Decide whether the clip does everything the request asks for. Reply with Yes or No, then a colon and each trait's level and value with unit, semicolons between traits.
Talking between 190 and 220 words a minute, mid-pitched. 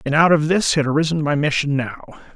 No: fast, 230 wpm; medium, 150 Hz